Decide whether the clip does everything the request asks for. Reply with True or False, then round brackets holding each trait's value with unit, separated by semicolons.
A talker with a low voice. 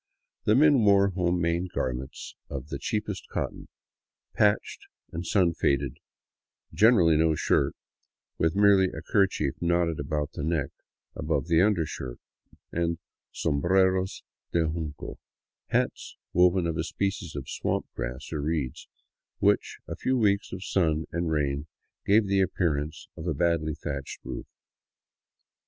True (85 Hz)